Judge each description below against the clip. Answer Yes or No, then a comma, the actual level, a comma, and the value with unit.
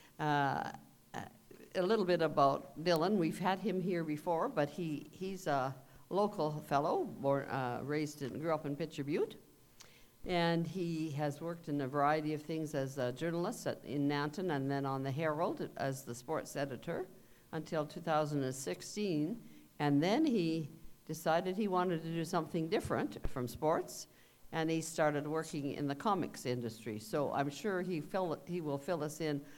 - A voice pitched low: No, medium, 155 Hz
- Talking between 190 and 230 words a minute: No, average, 180 wpm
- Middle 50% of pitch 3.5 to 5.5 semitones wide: No, average, 3.1 semitones